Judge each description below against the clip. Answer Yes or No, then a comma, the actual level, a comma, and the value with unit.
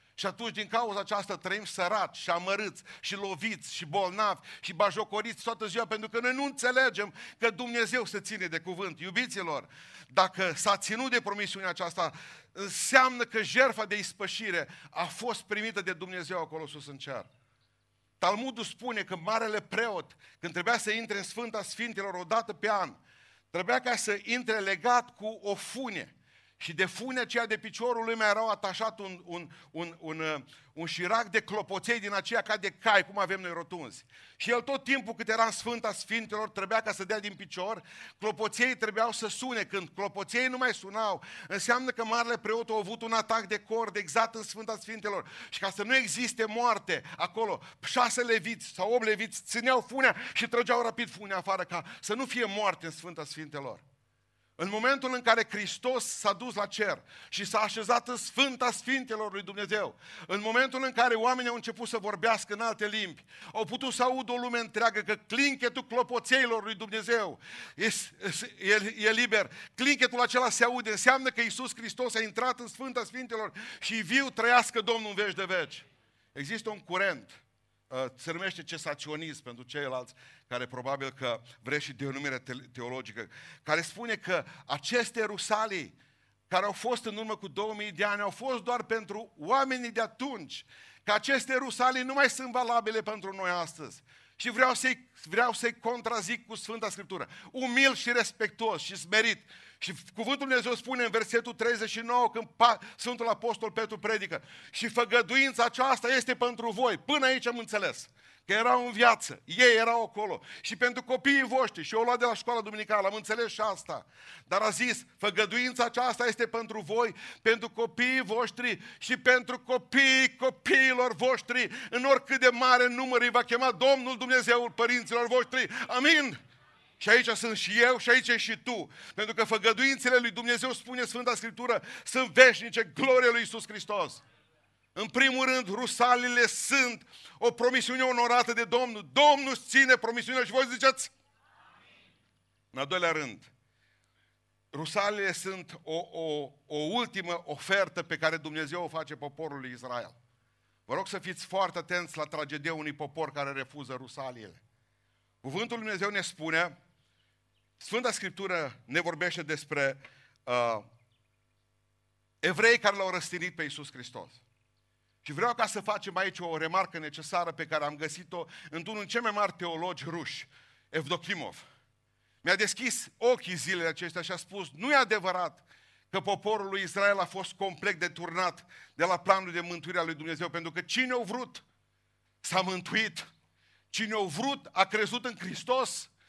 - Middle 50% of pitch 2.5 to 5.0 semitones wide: No, wide, 5.6 semitones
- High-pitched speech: Yes, high, 215 Hz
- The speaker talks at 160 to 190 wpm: Yes, average, 165 wpm